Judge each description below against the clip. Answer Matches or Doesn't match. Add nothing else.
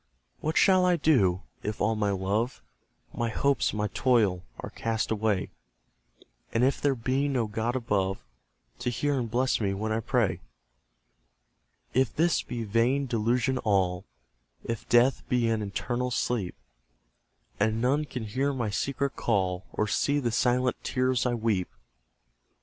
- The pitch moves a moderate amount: Matches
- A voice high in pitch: Doesn't match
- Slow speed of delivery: Doesn't match